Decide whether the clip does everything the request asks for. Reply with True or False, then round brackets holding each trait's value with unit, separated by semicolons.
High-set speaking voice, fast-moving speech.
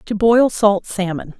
False (205 Hz; 170 wpm)